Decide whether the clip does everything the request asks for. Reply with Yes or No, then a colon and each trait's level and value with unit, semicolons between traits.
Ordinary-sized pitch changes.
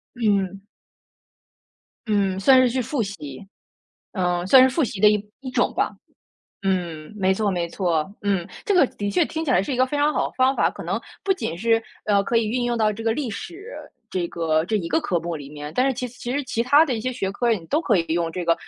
No: wide, 6.1 semitones